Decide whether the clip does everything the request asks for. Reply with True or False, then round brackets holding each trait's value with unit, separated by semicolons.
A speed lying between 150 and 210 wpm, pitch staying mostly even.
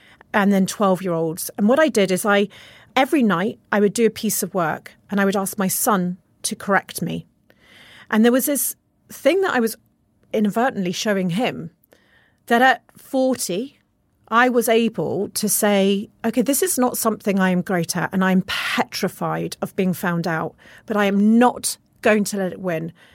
False (185 wpm; 3.9 semitones)